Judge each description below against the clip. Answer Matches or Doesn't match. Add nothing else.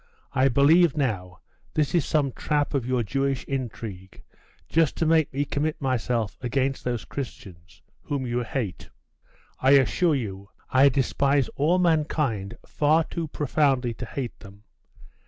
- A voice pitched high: Doesn't match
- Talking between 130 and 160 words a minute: Matches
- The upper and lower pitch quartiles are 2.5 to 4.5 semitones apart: Matches